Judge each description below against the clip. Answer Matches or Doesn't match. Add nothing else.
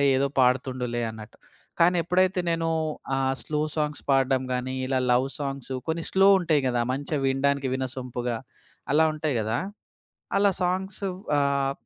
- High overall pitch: Doesn't match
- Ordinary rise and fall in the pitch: Matches